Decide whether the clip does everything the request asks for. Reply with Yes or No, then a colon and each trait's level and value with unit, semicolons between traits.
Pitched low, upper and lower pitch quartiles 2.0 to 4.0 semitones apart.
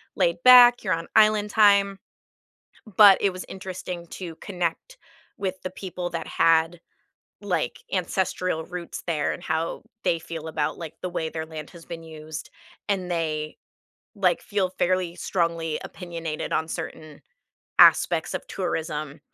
No: medium, 170 Hz; narrow, 2.6 semitones